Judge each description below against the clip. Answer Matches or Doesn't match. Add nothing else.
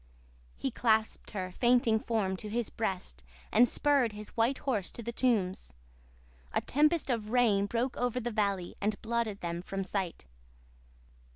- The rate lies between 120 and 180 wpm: Matches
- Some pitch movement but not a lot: Matches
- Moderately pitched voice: Doesn't match